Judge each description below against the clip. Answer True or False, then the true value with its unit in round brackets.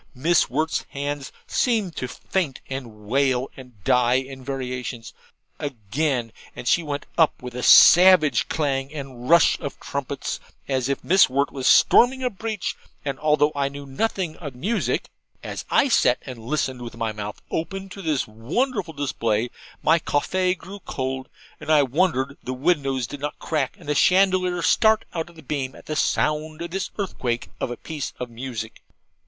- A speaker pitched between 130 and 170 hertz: True (140 Hz)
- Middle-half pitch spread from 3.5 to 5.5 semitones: True (4.9 semitones)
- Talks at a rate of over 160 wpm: True (170 wpm)